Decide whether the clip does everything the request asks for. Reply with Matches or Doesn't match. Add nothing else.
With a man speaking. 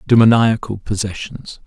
Matches